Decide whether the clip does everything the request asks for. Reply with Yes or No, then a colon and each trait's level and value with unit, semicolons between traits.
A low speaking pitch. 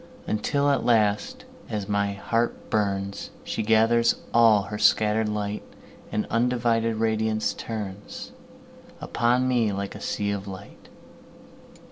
Yes: low, 110 Hz